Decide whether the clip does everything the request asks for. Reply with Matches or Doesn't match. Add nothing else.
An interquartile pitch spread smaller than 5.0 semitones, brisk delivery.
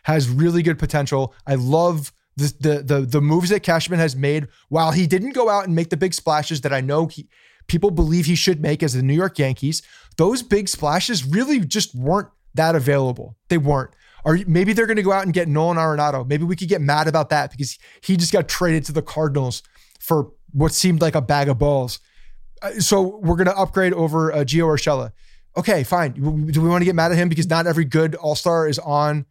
Matches